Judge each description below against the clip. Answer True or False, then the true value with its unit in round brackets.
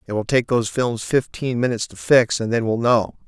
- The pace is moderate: False (240 wpm)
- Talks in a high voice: False (115 Hz)